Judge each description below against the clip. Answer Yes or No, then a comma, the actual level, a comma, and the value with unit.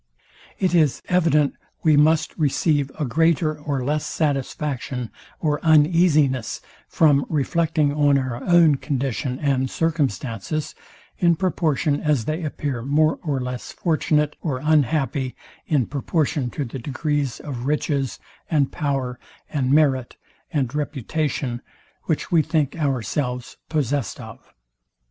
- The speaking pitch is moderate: Yes, medium, 145 Hz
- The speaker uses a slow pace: Yes, slow, 120 wpm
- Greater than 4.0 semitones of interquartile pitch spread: No, average, 2.8 semitones